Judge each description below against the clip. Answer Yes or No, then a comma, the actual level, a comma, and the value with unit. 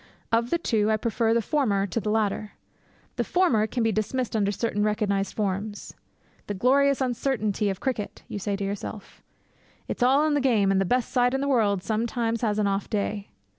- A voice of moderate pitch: No, high, 220 Hz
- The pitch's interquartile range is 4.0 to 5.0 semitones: No, average, 3.4 semitones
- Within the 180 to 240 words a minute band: Yes, average, 200 wpm